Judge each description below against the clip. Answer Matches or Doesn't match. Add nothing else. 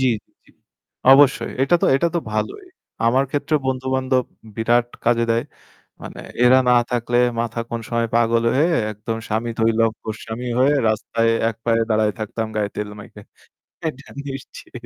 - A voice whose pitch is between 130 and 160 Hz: Doesn't match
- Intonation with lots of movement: Doesn't match